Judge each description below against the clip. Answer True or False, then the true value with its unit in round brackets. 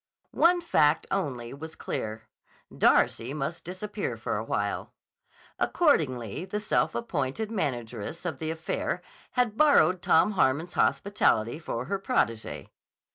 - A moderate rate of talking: False (125 wpm)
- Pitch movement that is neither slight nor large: False (7.8 semitones)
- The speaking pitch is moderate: True (160 Hz)